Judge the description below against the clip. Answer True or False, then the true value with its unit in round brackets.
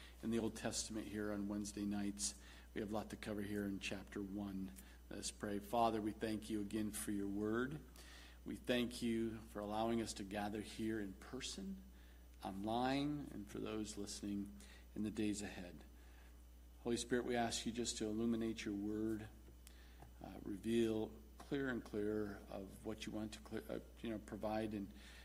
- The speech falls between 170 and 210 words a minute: True (180 wpm)